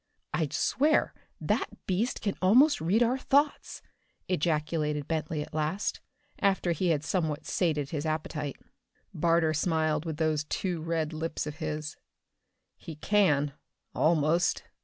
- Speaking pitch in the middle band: Yes, medium, 160 Hz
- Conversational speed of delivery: No, slow, 130 wpm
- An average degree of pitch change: Yes, average, 3.2 semitones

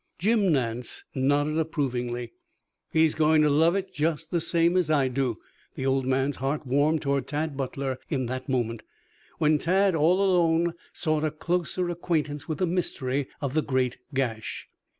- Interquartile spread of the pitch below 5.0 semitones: Yes, average, 3.7 semitones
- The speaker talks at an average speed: Yes, average, 165 wpm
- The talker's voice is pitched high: No, medium, 150 Hz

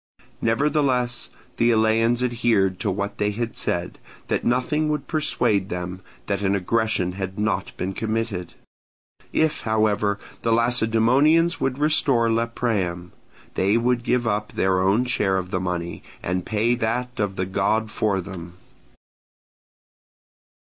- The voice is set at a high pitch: No, low, 110 Hz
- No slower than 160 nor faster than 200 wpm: No, slow, 135 wpm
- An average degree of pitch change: Yes, average, 4.0 semitones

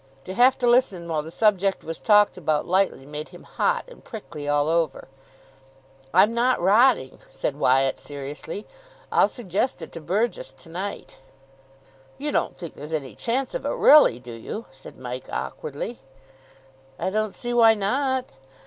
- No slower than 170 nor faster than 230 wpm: No, average, 160 wpm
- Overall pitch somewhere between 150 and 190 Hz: Yes, medium, 185 Hz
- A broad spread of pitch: Yes, wide, 7.9 semitones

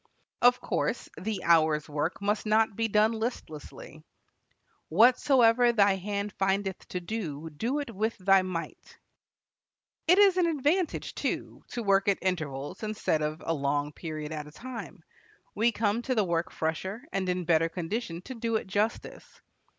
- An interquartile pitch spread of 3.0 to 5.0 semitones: No, wide, 5.6 semitones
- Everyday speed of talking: Yes, average, 160 wpm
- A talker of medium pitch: No, high, 200 Hz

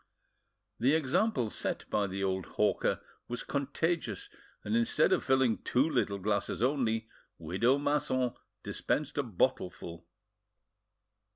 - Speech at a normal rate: No, slow, 115 wpm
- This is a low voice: Yes, low, 125 Hz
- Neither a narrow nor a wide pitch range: No, wide, 6.3 semitones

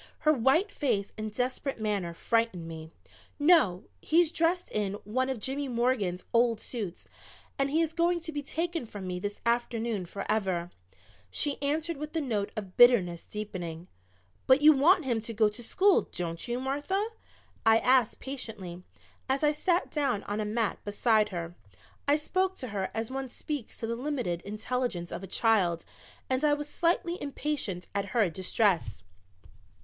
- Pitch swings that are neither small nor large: No, wide, 6.4 semitones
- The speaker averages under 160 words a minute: No, average, 165 wpm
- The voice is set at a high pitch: Yes, high, 235 Hz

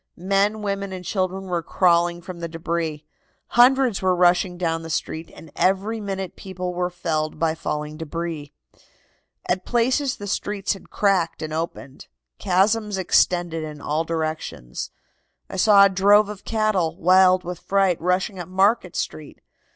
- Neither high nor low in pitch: Yes, medium, 180 Hz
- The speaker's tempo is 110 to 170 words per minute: Yes, average, 150 wpm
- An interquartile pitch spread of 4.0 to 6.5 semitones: No, average, 3.1 semitones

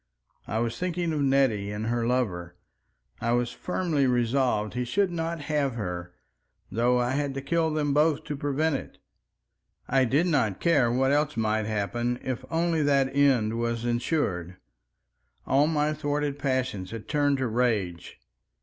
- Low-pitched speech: Yes, low, 130 Hz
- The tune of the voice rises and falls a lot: No, average, 4.4 semitones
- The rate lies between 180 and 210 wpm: No, average, 155 wpm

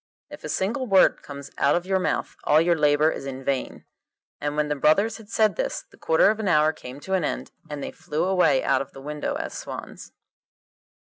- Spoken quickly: Yes, fast, 215 wpm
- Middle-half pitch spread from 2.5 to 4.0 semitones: No, average, 5.0 semitones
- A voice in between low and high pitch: Yes, medium, 160 Hz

